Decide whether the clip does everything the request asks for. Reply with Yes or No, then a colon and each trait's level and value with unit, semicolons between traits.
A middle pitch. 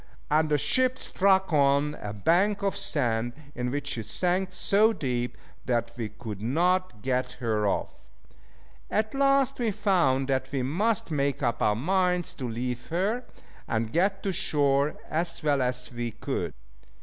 Yes: medium, 145 Hz